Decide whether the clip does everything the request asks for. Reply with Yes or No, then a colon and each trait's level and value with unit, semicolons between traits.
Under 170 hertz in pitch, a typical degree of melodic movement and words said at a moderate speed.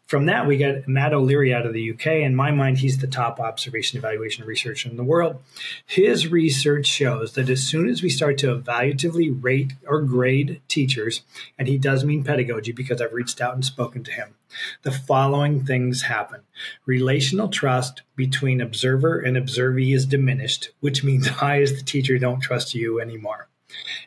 No: low, 135 Hz; narrow, 2.2 semitones; average, 180 wpm